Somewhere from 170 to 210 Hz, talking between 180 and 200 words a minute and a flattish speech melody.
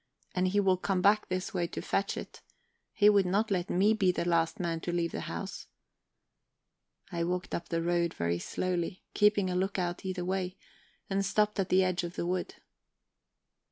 Yes: medium, 185 Hz; average, 190 wpm; narrow, 2.1 semitones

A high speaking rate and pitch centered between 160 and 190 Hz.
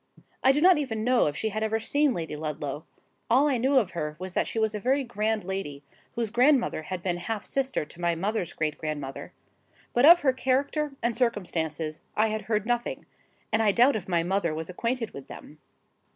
No: fast, 210 wpm; high, 215 Hz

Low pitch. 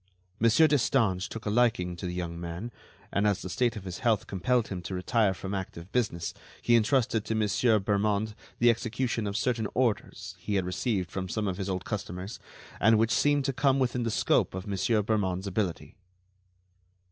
Yes: low, 105 Hz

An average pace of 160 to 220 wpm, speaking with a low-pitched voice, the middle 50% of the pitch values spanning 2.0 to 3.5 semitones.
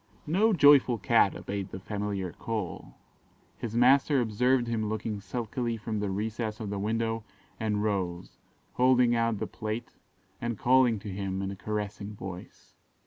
No: average, 150 wpm; low, 110 Hz; average, 3.0 semitones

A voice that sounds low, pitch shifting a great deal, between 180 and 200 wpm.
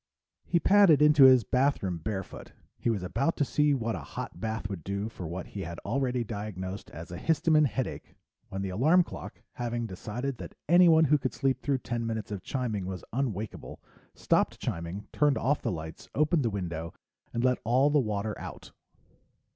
Yes: low, 115 Hz; wide, 6.1 semitones; average, 185 wpm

